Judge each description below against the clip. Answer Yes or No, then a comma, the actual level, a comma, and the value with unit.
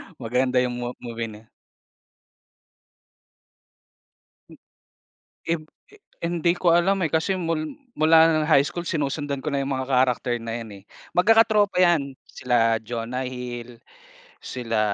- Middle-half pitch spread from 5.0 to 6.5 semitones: Yes, wide, 5.5 semitones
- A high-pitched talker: No, low, 135 Hz